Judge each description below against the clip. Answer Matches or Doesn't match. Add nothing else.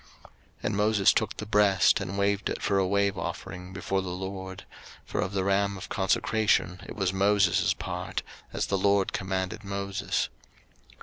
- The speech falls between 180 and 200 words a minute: Doesn't match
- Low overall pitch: Matches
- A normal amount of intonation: Doesn't match